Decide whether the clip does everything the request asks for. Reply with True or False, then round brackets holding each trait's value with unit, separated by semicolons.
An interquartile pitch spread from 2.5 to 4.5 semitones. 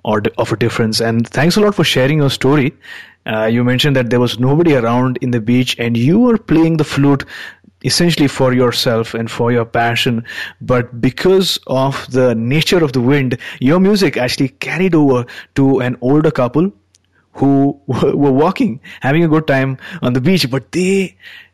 True (3.8 semitones)